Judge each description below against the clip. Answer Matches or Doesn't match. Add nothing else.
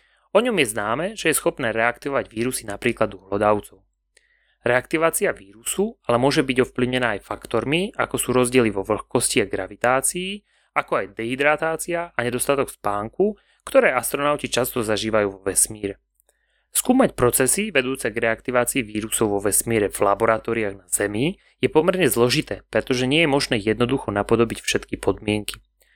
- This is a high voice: Doesn't match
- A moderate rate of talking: Matches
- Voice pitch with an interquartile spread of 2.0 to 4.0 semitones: Doesn't match